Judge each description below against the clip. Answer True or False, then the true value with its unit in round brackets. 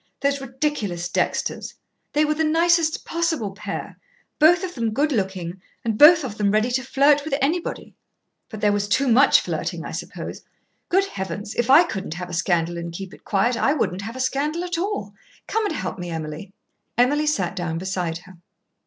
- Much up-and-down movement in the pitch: True (8.1 semitones)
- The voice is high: True (240 Hz)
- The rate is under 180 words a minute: False (190 wpm)